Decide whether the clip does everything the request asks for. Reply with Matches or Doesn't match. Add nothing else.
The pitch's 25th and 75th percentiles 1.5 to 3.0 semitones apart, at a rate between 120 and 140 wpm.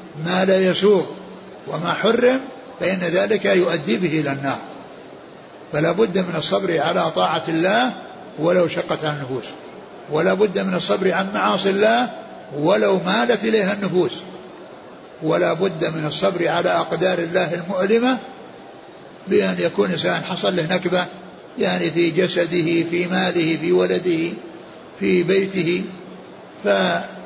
Matches